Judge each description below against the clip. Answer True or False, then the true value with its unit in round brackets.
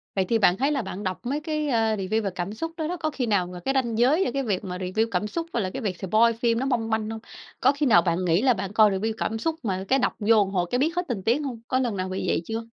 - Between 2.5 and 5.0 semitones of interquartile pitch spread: False (5.6 semitones)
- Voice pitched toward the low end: False (225 Hz)